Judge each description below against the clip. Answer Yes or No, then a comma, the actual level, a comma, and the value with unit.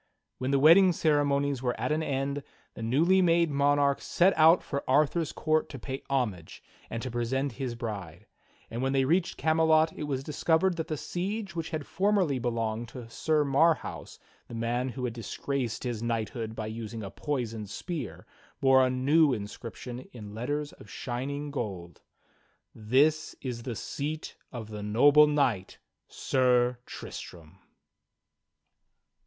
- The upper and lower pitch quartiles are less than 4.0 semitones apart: No, average, 4.8 semitones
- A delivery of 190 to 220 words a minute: No, average, 150 wpm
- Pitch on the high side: No, low, 135 Hz